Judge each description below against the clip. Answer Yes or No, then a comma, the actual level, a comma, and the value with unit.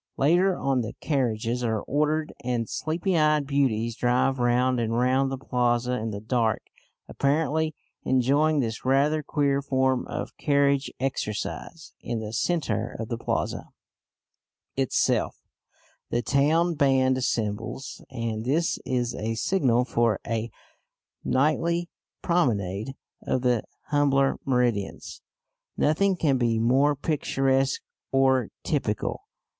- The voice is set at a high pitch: No, low, 130 Hz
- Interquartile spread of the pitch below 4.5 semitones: Yes, average, 3.6 semitones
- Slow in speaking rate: Yes, slow, 120 wpm